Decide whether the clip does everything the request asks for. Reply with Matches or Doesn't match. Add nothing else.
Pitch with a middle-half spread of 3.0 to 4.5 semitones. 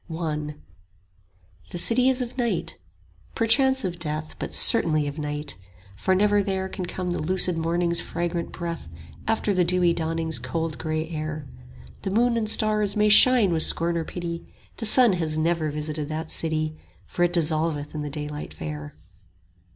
Matches